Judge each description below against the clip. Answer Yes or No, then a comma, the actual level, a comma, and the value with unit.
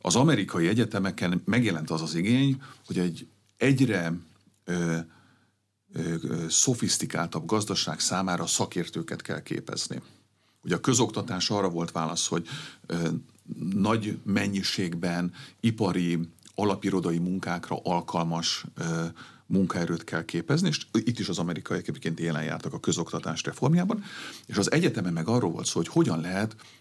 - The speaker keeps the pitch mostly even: No, average, 4.3 semitones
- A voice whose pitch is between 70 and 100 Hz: Yes, very low, 90 Hz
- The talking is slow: No, average, 130 wpm